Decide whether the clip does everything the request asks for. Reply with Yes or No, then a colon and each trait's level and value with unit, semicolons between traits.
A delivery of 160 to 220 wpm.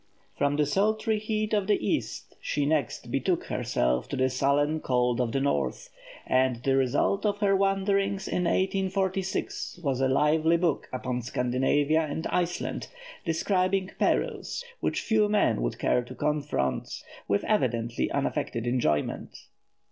No: average, 140 wpm